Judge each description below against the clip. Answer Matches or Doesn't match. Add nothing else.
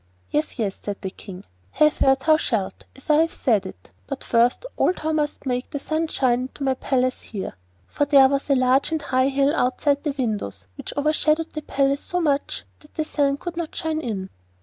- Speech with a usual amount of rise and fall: Matches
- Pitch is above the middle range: Matches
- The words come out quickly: Matches